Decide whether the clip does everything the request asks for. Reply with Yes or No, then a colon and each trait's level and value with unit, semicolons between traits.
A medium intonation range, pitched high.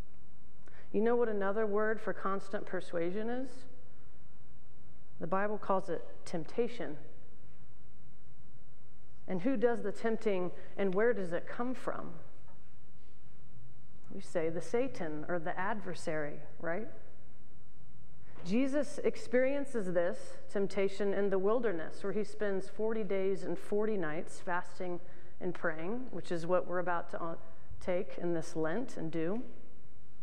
Yes: average, 4.1 semitones; high, 195 Hz